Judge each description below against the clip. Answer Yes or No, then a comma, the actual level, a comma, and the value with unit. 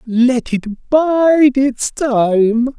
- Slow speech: Yes, slow, 110 wpm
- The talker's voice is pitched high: Yes, very high, 255 Hz